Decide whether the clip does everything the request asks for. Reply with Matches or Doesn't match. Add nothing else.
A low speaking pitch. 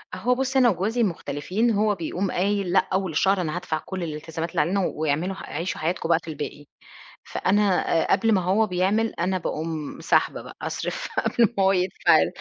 Doesn't match